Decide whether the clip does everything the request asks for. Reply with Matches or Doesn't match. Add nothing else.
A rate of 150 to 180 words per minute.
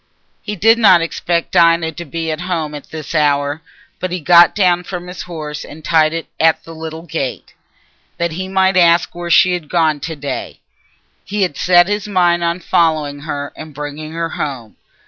Doesn't match